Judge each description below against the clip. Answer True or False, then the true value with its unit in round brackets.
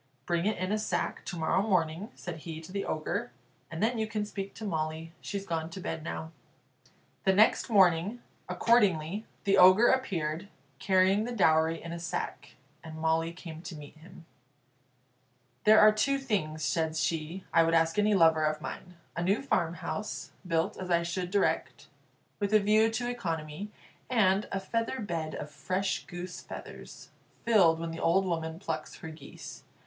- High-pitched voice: False (180 Hz)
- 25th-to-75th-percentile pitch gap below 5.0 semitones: True (4.2 semitones)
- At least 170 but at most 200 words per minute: True (175 wpm)